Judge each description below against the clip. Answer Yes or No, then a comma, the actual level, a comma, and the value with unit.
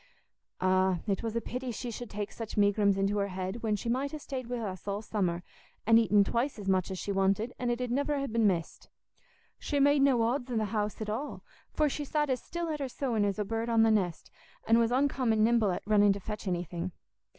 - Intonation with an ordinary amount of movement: Yes, average, 3.9 semitones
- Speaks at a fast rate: Yes, fast, 240 wpm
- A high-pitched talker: Yes, high, 220 Hz